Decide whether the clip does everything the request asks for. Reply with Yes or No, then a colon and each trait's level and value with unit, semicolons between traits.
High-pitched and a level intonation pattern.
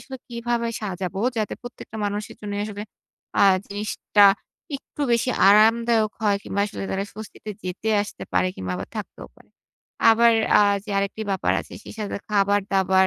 Yes: high, 210 Hz; narrow, 2.0 semitones